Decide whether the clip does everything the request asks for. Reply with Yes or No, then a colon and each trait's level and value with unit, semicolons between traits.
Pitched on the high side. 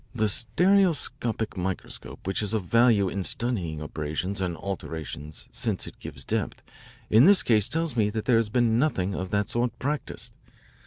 No: low, 110 Hz